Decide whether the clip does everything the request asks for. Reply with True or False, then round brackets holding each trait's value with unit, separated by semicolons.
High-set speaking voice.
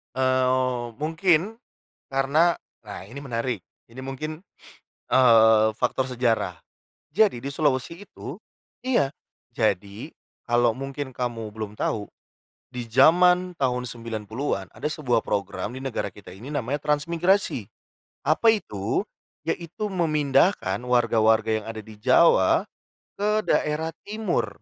False (130 Hz)